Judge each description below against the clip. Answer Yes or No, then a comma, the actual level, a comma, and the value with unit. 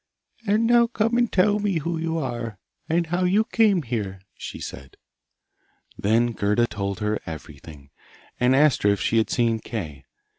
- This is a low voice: Yes, low, 120 Hz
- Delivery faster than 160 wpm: Yes, average, 170 wpm